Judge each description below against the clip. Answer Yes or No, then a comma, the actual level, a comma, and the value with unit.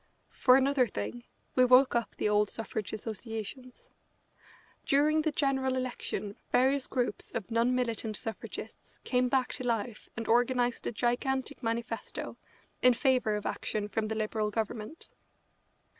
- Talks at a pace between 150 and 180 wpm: No, average, 140 wpm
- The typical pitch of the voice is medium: No, high, 240 Hz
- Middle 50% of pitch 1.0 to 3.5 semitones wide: Yes, average, 2.9 semitones